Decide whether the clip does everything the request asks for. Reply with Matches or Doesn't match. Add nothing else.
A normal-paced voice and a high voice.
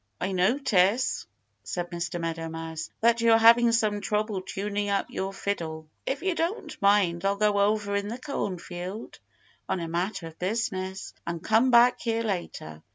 Matches